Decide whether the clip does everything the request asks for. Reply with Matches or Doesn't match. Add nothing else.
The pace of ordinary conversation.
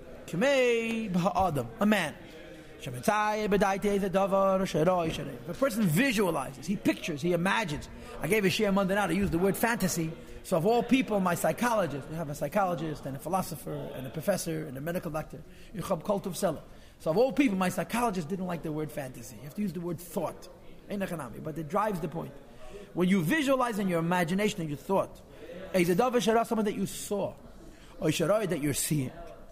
Matches